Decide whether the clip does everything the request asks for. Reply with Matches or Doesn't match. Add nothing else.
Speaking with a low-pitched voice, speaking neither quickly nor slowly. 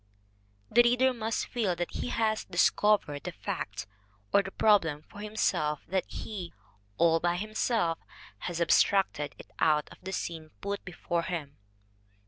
Doesn't match